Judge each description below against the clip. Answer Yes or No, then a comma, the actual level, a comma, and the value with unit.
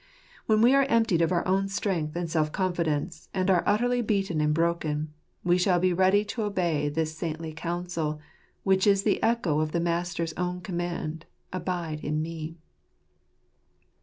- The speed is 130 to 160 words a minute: No, average, 170 wpm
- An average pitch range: Yes, average, 3.1 semitones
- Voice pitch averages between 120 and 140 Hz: No, medium, 175 Hz